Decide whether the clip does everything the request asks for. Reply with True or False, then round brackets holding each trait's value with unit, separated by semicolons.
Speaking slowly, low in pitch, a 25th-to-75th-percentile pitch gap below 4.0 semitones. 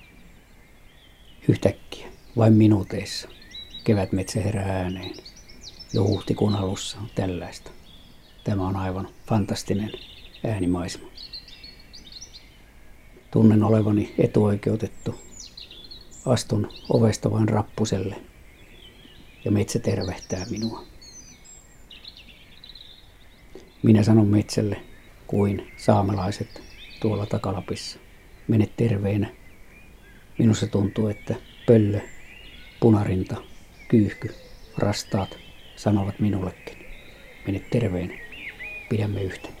True (75 wpm; 105 Hz; 2.4 semitones)